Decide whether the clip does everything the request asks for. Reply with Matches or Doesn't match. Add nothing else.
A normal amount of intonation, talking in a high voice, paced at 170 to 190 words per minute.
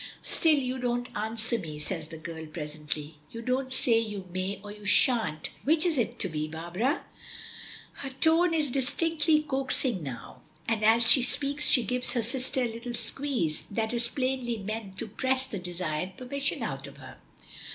Doesn't match